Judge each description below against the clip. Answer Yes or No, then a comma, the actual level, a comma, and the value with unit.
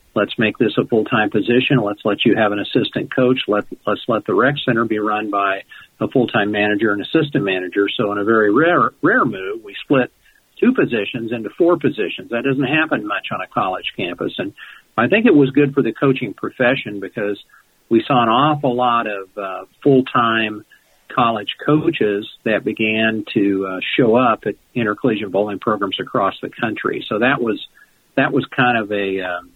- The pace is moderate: Yes, average, 190 wpm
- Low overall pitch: Yes, low, 115 Hz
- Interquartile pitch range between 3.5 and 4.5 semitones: Yes, average, 4.2 semitones